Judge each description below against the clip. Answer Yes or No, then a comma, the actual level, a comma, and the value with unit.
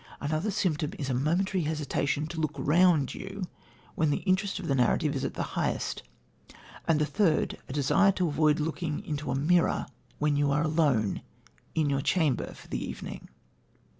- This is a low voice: No, medium, 155 Hz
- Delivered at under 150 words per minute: No, average, 175 wpm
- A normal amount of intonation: Yes, average, 3.3 semitones